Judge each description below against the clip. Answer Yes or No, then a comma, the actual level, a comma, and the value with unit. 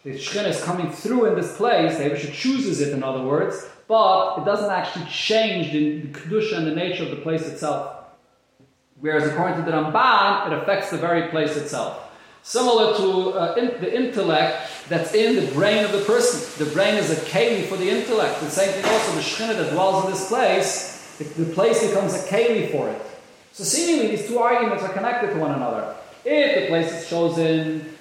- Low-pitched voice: No, medium, 180 Hz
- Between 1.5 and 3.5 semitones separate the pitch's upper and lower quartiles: No, wide, 5.6 semitones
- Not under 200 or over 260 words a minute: Yes, fast, 205 wpm